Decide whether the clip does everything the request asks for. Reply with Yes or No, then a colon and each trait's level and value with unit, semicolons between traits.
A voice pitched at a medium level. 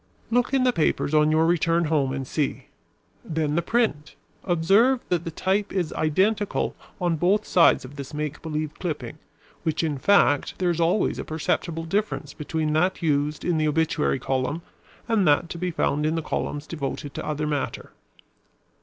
Yes: medium, 160 Hz